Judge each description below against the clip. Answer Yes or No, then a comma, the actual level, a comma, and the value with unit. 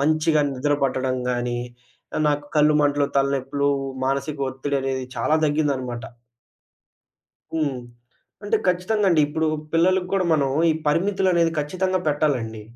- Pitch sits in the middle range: Yes, medium, 145 Hz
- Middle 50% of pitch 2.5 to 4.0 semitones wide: Yes, average, 3.5 semitones